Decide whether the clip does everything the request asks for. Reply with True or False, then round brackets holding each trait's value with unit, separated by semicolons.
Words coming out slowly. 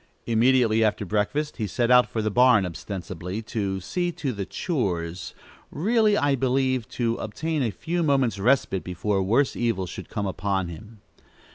False (160 wpm)